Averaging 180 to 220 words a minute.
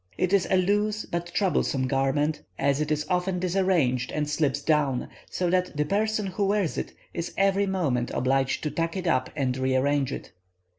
Yes: average, 185 wpm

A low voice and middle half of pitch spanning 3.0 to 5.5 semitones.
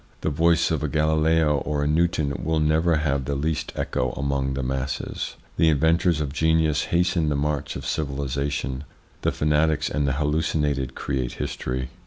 No: very low, 75 Hz; narrow, 2.4 semitones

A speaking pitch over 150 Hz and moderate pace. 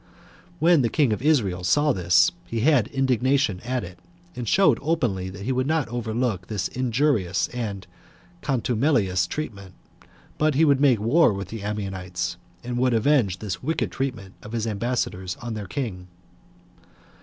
No: low, 115 Hz; average, 155 wpm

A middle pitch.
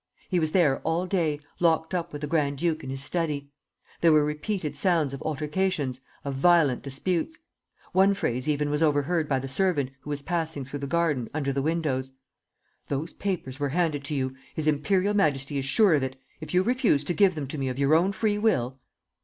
Yes: medium, 150 Hz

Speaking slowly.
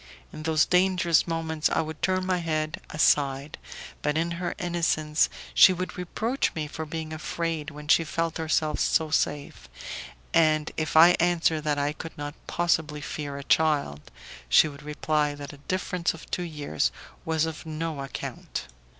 No: average, 165 wpm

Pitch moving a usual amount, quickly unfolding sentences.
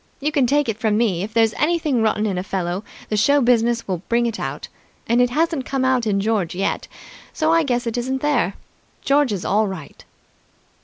Yes: average, 4.5 semitones; fast, 210 wpm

